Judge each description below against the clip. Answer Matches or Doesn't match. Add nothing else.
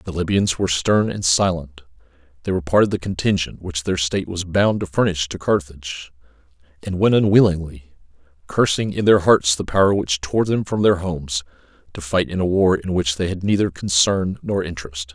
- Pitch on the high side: Doesn't match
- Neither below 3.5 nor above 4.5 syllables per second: Doesn't match